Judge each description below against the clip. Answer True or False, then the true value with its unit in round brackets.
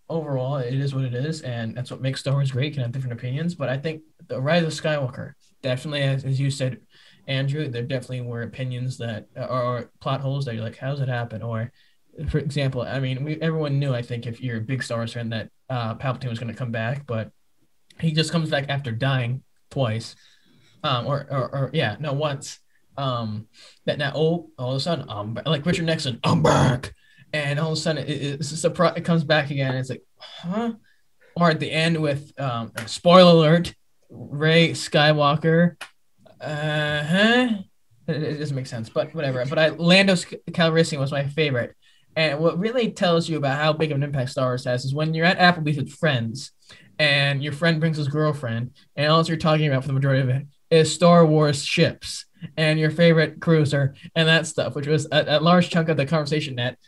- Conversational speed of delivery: False (210 wpm)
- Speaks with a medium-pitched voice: True (145 Hz)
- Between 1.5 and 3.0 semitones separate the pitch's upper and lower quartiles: False (3.9 semitones)